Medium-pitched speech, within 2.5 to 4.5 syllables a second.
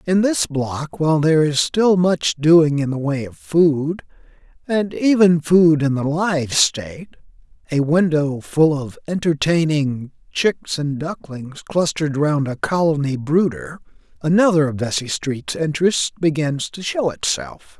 Yes: medium, 155 Hz; 4.1 syllables/s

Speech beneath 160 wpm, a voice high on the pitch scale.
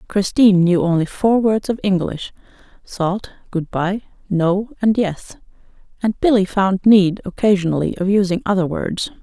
Yes: average, 145 wpm; high, 195 Hz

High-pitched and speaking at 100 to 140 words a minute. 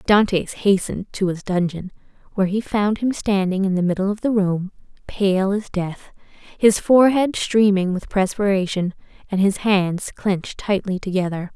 No: high, 195 Hz; average, 155 wpm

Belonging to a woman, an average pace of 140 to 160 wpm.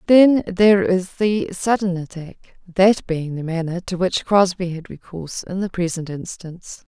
Yes: female; average, 155 wpm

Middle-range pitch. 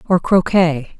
Yes: medium, 170 Hz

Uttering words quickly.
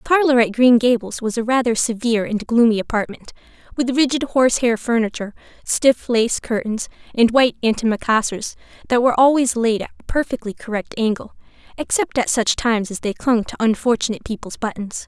No: average, 165 wpm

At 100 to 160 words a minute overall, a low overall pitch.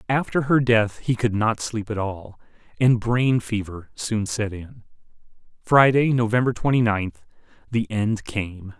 Yes: average, 150 wpm; low, 110 Hz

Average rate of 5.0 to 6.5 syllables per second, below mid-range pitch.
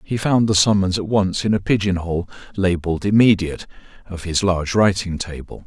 Yes: 5.5 syllables/s; very low, 95 Hz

